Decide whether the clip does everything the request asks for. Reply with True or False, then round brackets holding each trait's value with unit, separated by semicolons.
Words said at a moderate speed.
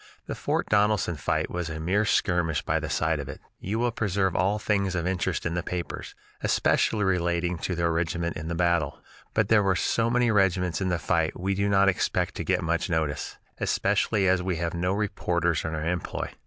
False (210 wpm)